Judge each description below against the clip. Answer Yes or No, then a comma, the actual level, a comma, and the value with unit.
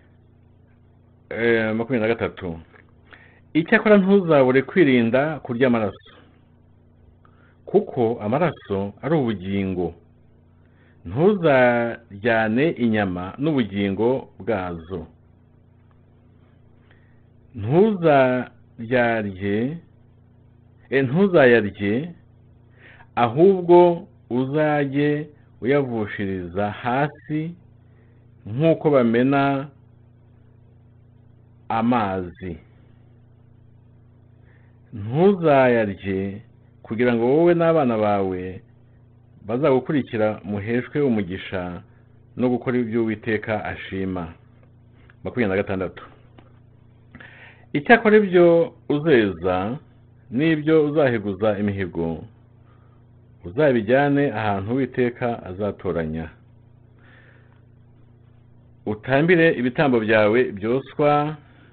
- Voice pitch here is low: Yes, low, 120 Hz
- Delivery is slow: Yes, slow, 55 wpm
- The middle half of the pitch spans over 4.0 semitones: No, average, 2.7 semitones